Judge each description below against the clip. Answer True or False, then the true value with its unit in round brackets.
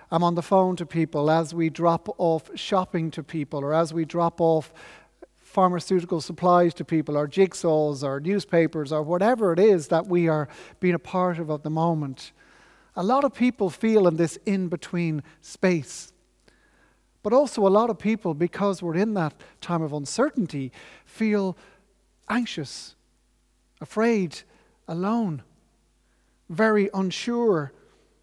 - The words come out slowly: False (145 wpm)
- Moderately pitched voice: True (175 Hz)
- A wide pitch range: False (3.6 semitones)